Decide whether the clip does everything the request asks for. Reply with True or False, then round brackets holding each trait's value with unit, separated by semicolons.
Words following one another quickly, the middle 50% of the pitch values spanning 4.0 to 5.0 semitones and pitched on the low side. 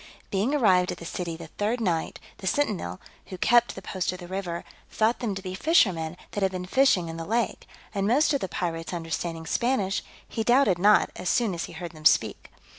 False (215 wpm; 4.6 semitones; 190 Hz)